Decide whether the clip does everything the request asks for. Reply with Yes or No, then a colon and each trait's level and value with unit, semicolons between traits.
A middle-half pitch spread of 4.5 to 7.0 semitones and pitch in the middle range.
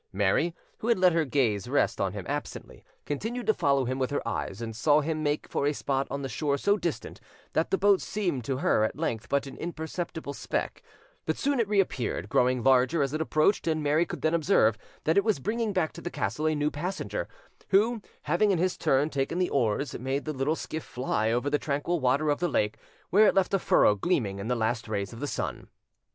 Yes: average, 5.3 semitones; medium, 150 Hz